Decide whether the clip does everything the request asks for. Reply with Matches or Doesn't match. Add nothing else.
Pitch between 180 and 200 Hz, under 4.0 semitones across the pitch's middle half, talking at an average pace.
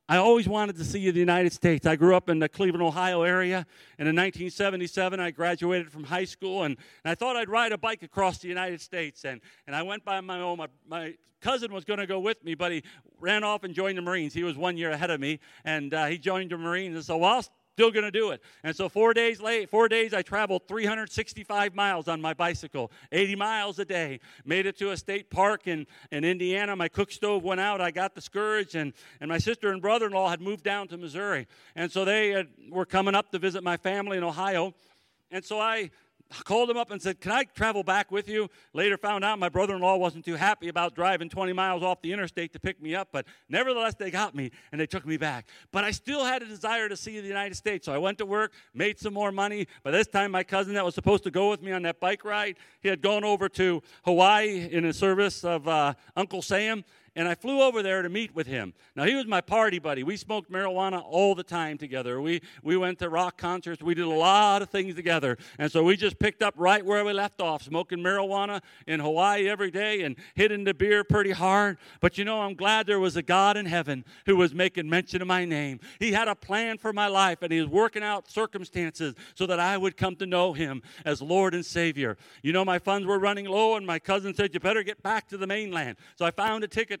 Doesn't match